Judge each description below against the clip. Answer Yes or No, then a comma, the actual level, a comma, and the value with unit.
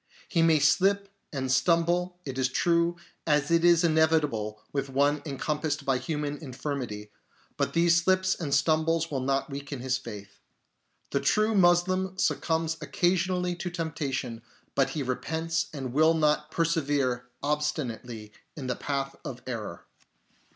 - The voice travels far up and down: No, average, 3.8 semitones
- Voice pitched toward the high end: No, medium, 150 Hz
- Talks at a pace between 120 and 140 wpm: Yes, slow, 135 wpm